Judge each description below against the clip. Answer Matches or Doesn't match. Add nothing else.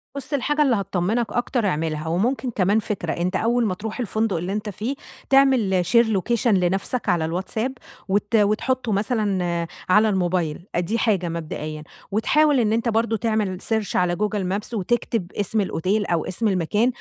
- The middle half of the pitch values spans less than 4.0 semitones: Doesn't match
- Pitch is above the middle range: Matches